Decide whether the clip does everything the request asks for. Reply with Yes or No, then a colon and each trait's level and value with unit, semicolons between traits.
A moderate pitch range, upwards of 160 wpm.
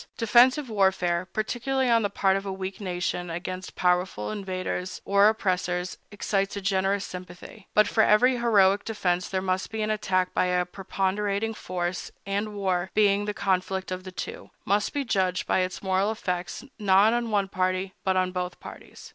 No: narrow, 2.3 semitones; average, 175 wpm